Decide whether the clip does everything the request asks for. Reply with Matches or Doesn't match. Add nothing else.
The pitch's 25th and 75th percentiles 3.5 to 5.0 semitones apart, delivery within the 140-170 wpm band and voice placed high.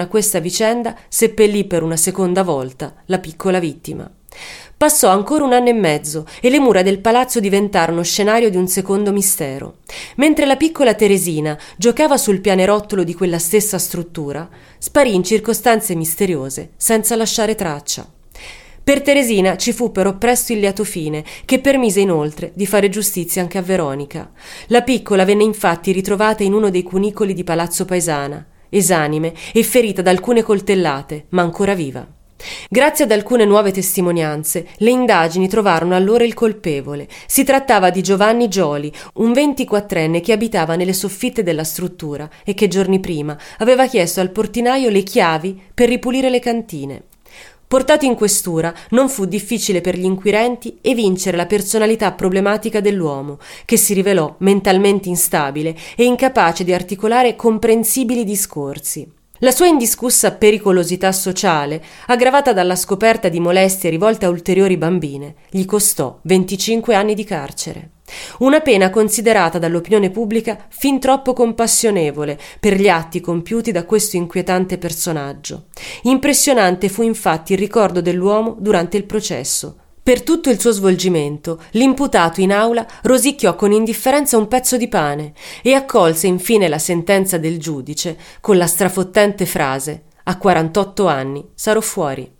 Matches